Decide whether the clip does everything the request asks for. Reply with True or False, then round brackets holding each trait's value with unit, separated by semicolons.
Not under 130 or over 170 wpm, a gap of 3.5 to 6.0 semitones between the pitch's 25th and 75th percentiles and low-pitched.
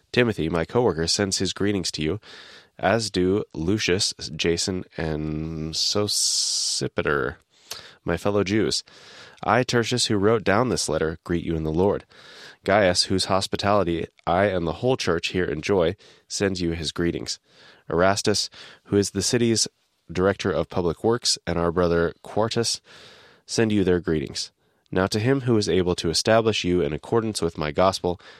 True (160 wpm; 3.9 semitones; 95 Hz)